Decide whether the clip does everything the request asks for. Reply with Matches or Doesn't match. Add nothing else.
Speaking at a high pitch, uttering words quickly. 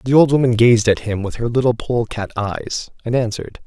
Doesn't match